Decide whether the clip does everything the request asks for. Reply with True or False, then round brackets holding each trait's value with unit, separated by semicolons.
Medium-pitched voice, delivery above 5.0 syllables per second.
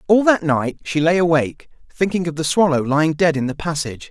True (160 Hz; 6.0 syllables/s)